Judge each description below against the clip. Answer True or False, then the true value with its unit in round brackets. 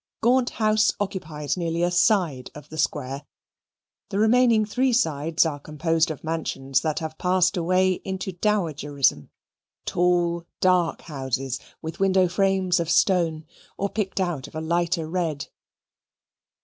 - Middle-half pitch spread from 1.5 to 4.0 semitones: True (3.5 semitones)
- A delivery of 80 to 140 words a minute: True (135 wpm)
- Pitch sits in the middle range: True (170 Hz)